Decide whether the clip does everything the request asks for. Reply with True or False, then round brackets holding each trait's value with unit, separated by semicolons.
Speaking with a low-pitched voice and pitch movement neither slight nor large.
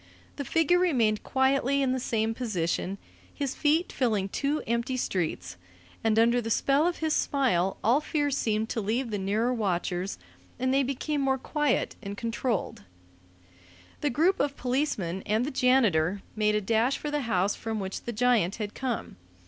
False (235 Hz; 4.7 semitones)